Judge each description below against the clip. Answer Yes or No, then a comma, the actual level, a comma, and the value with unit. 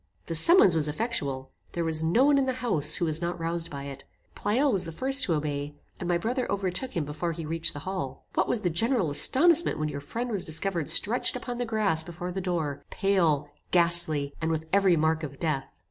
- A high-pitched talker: No, medium, 170 Hz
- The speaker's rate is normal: No, fast, 220 wpm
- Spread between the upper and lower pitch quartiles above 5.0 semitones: Yes, wide, 5.4 semitones